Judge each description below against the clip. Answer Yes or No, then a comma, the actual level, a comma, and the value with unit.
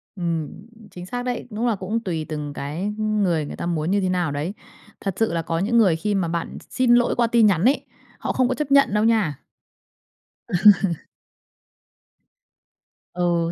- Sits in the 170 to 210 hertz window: Yes, high, 190 Hz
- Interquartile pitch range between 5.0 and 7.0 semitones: Yes, wide, 5.4 semitones